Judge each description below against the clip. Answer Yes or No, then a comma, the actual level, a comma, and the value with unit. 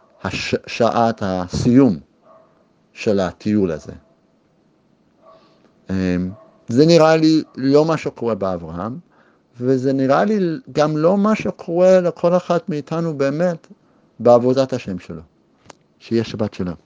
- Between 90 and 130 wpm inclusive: Yes, average, 105 wpm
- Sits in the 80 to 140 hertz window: Yes, low, 135 Hz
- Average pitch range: No, wide, 7.6 semitones